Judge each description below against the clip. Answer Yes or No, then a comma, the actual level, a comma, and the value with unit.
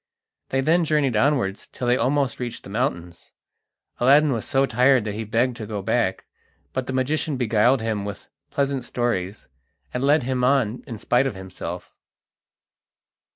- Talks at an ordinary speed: Yes, average, 160 wpm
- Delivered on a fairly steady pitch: No, average, 3.9 semitones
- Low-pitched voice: Yes, low, 125 Hz